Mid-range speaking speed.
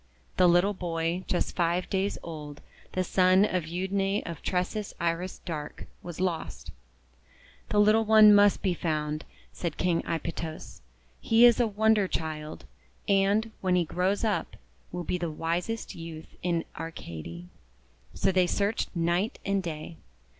Yes: average, 145 wpm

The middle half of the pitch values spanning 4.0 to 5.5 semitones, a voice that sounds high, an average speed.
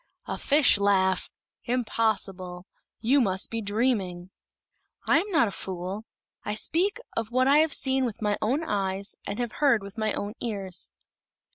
Yes: average, 4.8 semitones; high, 215 Hz; average, 160 wpm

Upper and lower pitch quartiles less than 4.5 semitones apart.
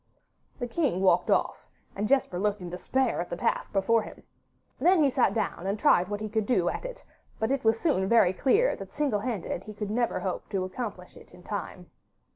No: average, 4.9 semitones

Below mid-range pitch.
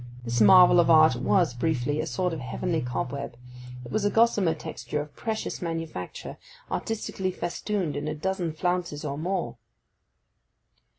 No: medium, 165 Hz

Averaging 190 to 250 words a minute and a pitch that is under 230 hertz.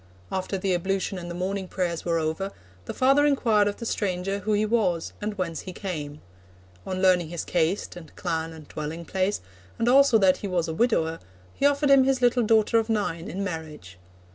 Yes: average, 200 wpm; high, 190 Hz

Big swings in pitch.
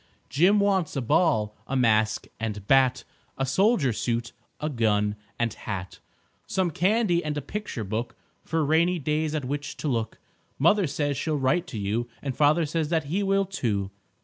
Yes: wide, 6.6 semitones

